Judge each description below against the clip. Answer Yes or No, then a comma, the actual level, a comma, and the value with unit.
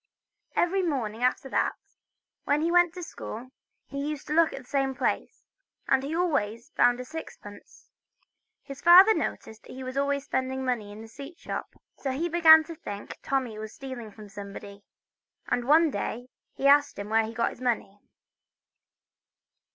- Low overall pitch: No, very high, 265 Hz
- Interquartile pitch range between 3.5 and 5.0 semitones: No, wide, 5.4 semitones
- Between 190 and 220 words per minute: No, average, 170 wpm